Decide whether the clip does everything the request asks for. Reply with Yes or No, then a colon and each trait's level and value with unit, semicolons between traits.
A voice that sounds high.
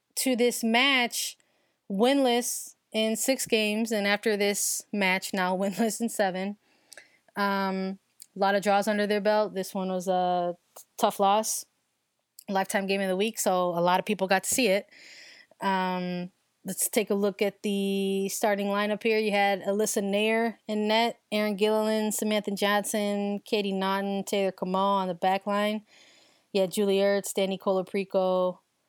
Yes: high, 205 Hz